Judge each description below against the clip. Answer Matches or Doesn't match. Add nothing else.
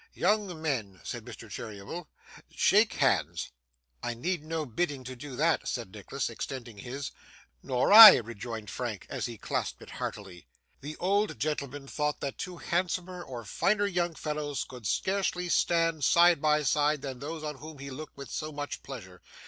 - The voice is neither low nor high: Matches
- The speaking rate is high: Doesn't match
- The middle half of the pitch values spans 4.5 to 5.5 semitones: Matches